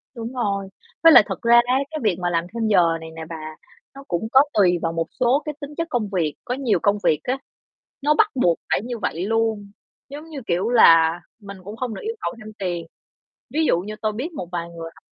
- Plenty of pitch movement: Yes, wide, 6.4 semitones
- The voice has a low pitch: No, high, 215 Hz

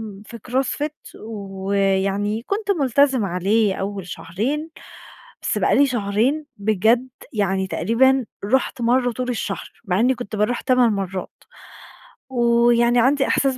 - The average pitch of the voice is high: Yes, high, 230 Hz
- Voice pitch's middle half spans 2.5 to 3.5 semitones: No, average, 4.5 semitones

